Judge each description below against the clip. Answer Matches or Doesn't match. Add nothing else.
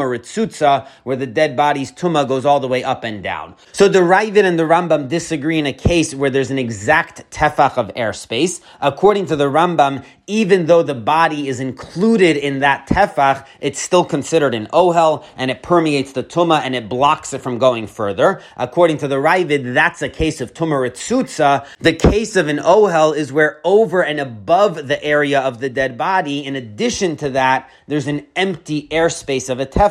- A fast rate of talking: Doesn't match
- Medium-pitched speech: Matches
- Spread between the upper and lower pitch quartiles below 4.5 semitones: Matches